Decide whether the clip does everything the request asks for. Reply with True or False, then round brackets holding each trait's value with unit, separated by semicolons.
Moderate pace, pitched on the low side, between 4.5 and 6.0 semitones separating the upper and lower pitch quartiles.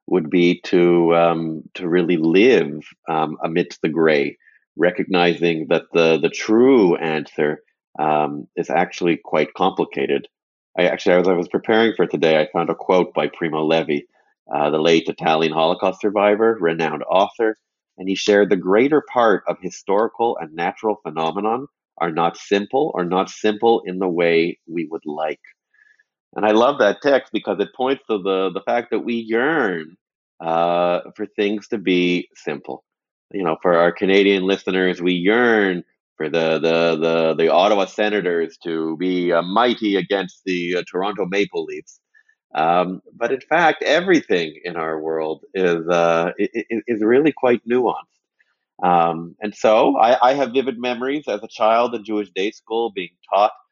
True (160 wpm; 95 Hz; 4.9 semitones)